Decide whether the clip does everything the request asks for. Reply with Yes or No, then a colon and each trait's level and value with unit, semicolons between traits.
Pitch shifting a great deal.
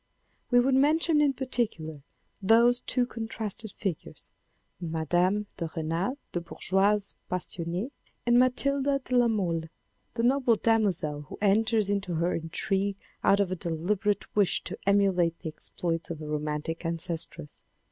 Yes: wide, 5.8 semitones